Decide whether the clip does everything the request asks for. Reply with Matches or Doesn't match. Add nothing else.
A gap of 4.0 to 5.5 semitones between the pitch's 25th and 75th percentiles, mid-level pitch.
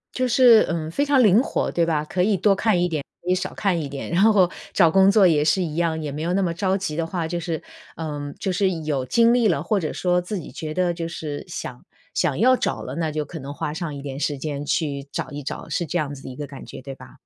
Matches